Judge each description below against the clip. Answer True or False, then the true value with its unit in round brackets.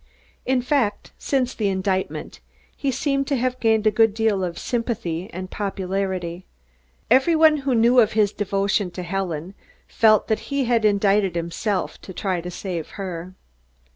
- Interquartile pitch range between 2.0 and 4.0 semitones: False (4.4 semitones)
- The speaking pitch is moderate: False (205 Hz)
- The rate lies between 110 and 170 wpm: True (160 wpm)